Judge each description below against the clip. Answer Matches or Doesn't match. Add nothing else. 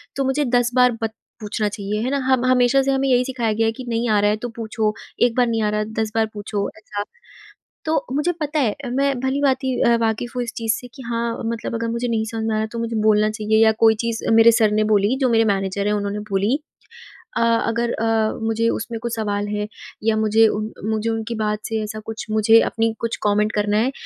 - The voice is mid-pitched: Doesn't match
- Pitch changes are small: Matches